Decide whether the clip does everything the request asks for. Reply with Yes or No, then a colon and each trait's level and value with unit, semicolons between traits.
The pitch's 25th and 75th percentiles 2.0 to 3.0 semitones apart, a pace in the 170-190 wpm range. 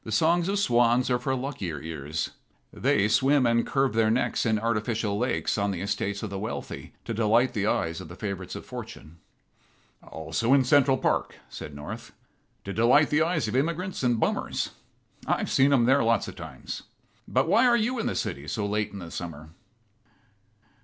No: average, 5.1 semitones; average, 185 wpm